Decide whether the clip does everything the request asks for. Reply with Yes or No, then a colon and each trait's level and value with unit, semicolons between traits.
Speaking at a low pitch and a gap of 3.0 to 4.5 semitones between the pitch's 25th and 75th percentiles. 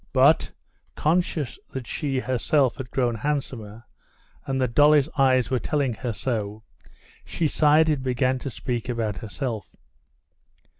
Yes: low, 130 Hz; average, 3.8 semitones